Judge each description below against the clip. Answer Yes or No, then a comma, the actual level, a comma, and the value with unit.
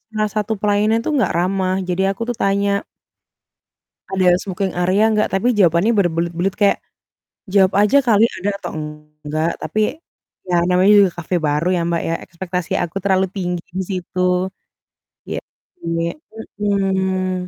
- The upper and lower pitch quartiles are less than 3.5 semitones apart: Yes, narrow, 2.5 semitones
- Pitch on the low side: No, high, 190 Hz